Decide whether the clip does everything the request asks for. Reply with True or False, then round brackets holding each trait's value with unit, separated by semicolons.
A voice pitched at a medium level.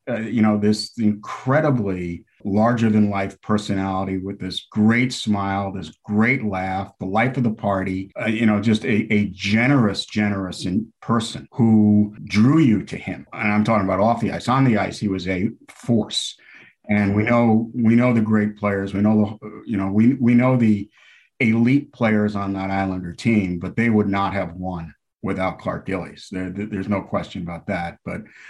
False (105 Hz)